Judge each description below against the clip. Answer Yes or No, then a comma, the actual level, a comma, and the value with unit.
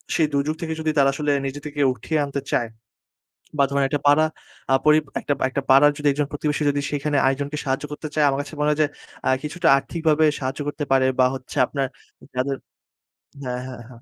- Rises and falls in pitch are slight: Yes, narrow, 1.8 semitones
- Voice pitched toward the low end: No, medium, 145 Hz